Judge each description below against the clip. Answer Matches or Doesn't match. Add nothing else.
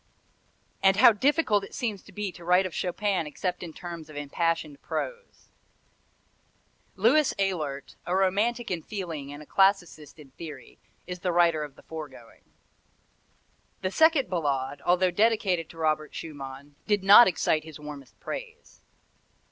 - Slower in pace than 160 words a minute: Matches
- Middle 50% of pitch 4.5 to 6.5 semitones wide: Matches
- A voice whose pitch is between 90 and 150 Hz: Doesn't match